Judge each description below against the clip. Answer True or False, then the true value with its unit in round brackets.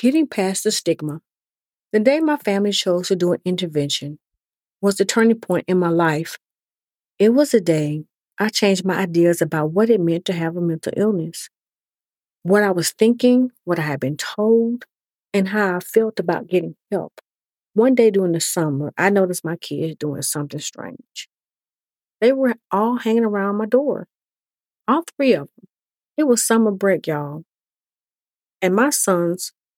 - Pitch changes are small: False (5.2 semitones)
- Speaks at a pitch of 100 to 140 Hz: False (195 Hz)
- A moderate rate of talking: True (170 wpm)